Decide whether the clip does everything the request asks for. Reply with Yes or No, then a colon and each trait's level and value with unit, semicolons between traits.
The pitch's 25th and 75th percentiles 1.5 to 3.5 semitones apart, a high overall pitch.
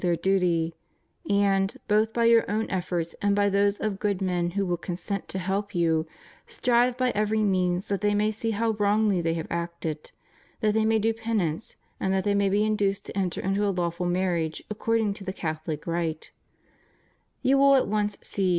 Yes: average, 3.2 semitones; high, 200 Hz